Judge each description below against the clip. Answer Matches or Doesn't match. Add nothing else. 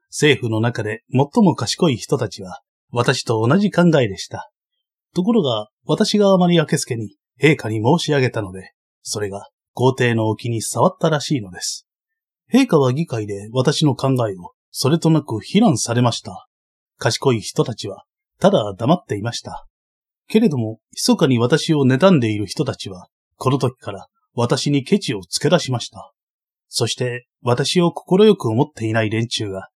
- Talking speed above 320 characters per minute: Doesn't match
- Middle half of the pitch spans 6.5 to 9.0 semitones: Matches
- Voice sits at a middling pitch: Doesn't match